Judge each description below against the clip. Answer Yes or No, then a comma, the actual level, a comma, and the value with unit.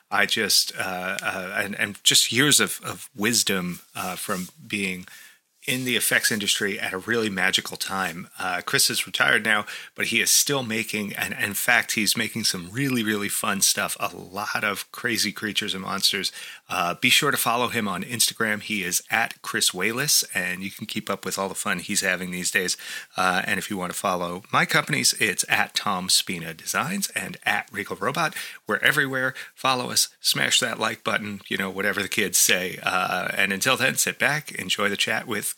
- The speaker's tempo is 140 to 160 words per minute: No, average, 200 wpm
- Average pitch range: Yes, average, 3.1 semitones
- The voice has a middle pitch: No, low, 100 Hz